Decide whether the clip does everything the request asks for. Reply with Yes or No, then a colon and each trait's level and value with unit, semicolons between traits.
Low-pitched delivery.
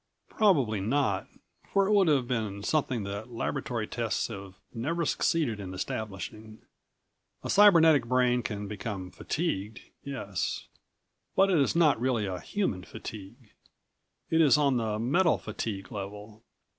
Yes: low, 115 Hz